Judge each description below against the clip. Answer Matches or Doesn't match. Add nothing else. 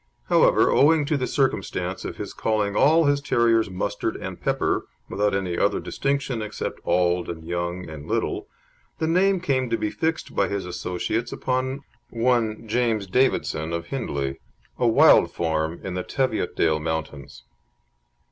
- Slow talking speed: Doesn't match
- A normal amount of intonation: Doesn't match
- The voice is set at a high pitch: Doesn't match